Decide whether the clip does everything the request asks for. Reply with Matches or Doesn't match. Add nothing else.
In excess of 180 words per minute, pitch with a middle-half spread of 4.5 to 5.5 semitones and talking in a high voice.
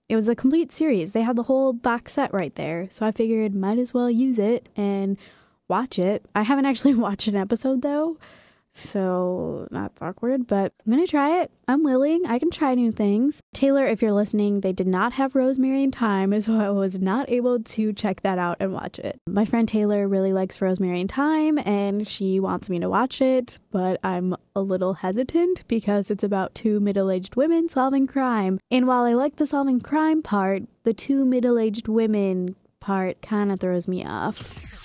Matches